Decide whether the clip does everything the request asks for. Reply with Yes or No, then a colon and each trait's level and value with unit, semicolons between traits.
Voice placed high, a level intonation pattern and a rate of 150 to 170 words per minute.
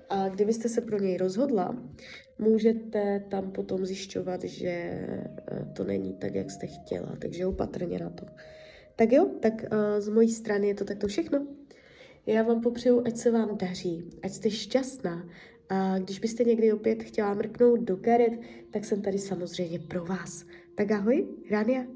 No: high, 210 Hz; average, 3.5 semitones; average, 160 wpm